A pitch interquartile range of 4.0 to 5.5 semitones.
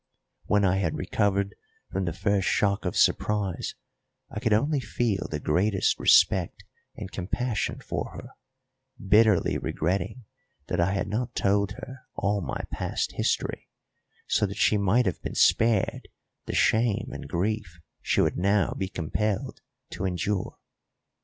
No: narrow, 2.4 semitones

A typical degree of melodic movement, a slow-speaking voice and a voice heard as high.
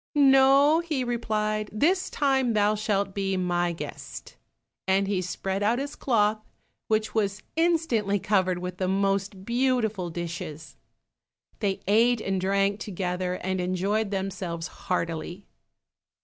Yes: average, 3.7 semitones; slow, 125 wpm; high, 200 Hz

